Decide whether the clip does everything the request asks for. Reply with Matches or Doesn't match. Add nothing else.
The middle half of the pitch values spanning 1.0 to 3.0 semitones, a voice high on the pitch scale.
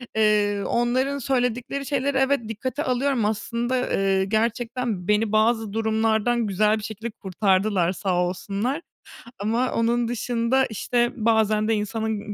Matches